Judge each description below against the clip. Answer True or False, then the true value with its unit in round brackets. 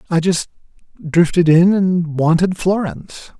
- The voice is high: False (170 Hz)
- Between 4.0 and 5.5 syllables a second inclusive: True (4.5 syllables/s)